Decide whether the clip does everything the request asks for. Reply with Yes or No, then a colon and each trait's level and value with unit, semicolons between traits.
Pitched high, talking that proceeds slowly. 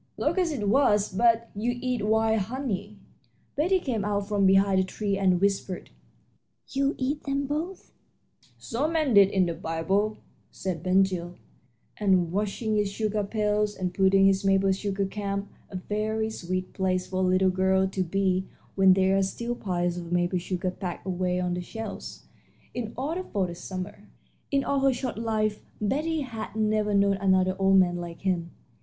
No: high, 200 Hz; average, 175 wpm